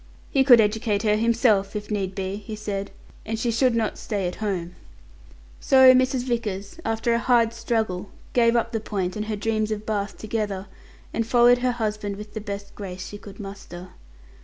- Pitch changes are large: No, narrow, 2.5 semitones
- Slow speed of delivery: No, average, 185 wpm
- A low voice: No, high, 215 Hz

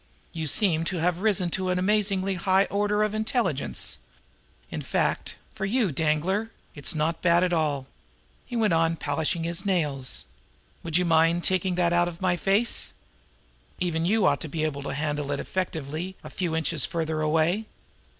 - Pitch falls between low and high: Yes, medium, 175 Hz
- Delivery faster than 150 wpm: Yes, average, 180 wpm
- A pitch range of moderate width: Yes, average, 3.2 semitones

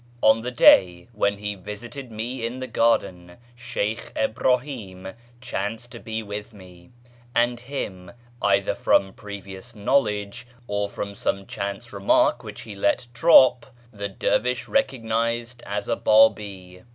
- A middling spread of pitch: Yes, average, 3.2 semitones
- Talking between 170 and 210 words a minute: No, slow, 135 wpm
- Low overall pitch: Yes, low, 105 Hz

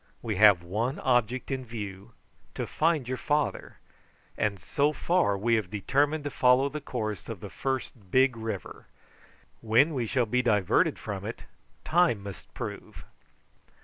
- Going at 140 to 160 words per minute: Yes, average, 150 wpm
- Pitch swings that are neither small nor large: Yes, average, 4.6 semitones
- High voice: No, low, 120 Hz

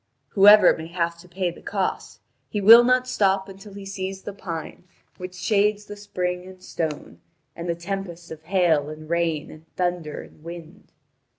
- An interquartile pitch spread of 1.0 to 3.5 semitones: Yes, average, 2.7 semitones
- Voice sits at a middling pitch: Yes, medium, 180 Hz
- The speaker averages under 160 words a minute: No, average, 175 wpm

